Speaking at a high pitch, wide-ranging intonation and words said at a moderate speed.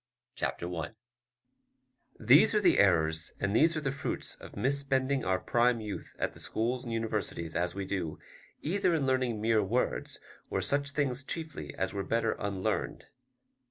No: low, 115 Hz; wide, 5.9 semitones; average, 160 wpm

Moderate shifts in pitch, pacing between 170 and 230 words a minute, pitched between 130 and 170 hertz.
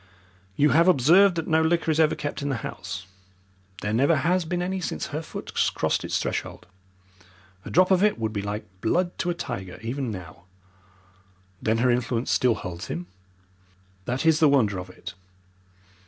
No: wide, 8.0 semitones; average, 180 wpm; low, 135 Hz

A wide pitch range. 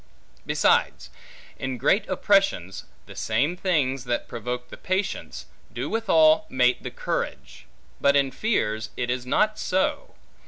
Yes: wide, 7.2 semitones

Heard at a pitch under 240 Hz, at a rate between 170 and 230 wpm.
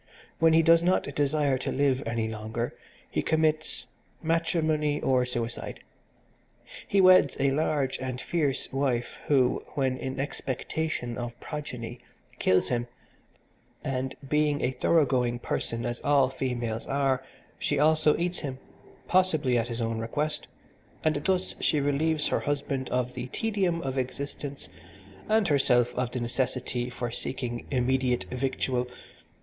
No: low, 135 Hz; average, 140 wpm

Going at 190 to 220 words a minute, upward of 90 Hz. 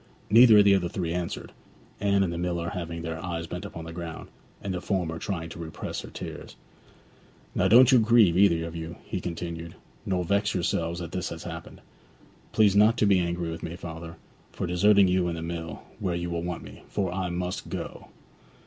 No: average, 200 wpm; very low, 85 Hz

